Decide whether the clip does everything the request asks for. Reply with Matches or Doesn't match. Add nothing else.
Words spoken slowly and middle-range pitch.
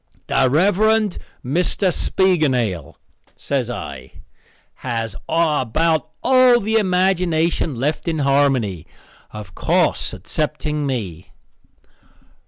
Matches